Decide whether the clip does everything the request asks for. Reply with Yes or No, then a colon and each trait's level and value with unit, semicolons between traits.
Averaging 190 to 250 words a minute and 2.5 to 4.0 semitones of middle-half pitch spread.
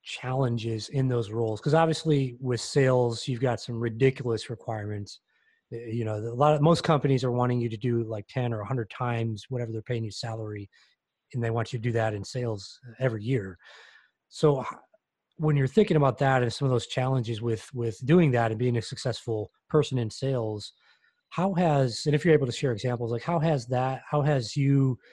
Yes: average, 200 wpm; average, 2.9 semitones